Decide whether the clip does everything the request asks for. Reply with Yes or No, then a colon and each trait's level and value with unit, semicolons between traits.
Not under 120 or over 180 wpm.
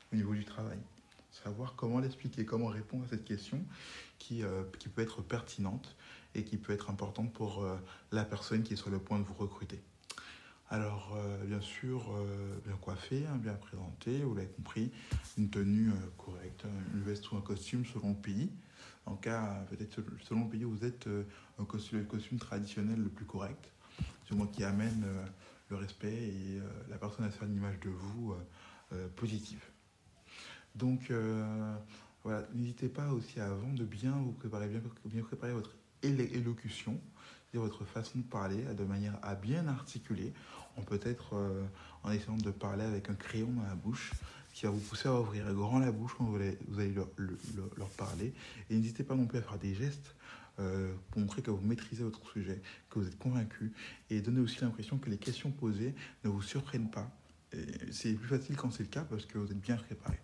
No: average, 205 wpm